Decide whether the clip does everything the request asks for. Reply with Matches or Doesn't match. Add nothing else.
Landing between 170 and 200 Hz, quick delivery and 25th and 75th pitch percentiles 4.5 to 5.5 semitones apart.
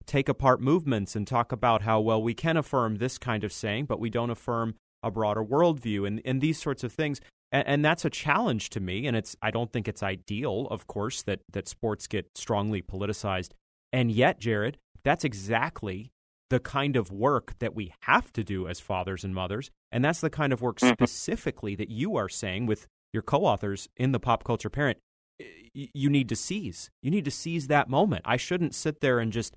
Doesn't match